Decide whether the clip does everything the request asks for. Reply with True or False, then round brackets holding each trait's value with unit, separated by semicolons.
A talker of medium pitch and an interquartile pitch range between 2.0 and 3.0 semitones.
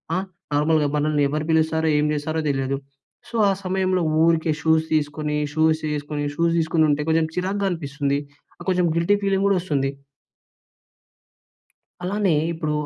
True (160 Hz; 2.6 semitones)